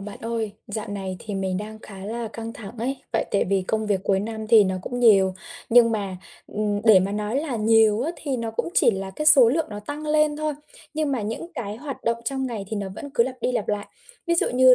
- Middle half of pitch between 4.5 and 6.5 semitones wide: No, average, 3.7 semitones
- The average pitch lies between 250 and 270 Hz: No, high, 220 Hz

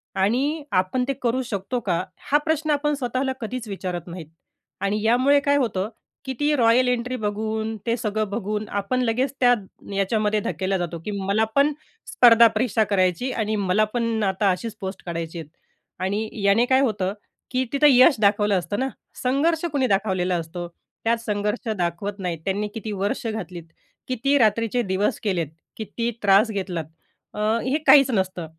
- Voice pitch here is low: No, high, 215 Hz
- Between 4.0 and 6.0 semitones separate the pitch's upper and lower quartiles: Yes, average, 4.6 semitones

